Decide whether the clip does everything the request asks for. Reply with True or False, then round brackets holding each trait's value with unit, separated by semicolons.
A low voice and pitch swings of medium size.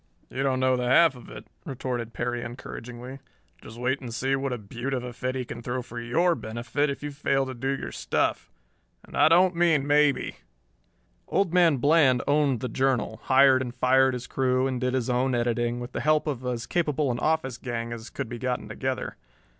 False (130 Hz; 2.3 semitones)